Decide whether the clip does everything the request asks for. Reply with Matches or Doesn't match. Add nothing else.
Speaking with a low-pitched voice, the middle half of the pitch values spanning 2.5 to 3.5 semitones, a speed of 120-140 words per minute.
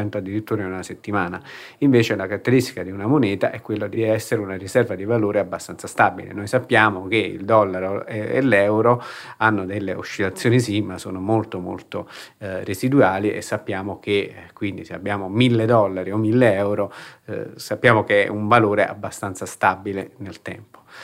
Doesn't match